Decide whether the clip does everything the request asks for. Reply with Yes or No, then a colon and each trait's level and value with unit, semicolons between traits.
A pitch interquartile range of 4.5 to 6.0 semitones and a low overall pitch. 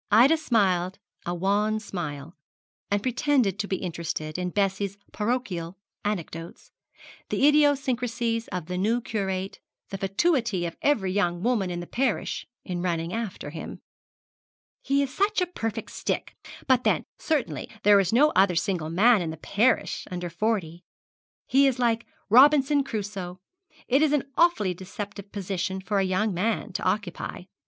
No: average, 5.2 semitones; high, 205 Hz